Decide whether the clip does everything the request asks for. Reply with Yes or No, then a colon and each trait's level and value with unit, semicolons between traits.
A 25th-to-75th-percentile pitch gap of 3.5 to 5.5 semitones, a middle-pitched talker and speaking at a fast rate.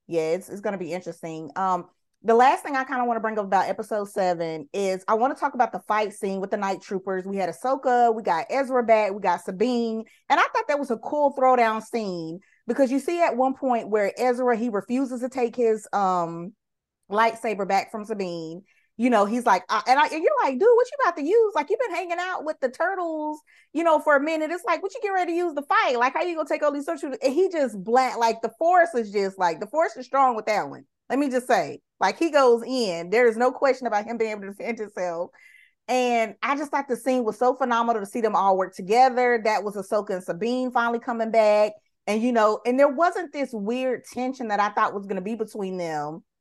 No: average, 5.0 semitones; high, 235 Hz; fast, 250 wpm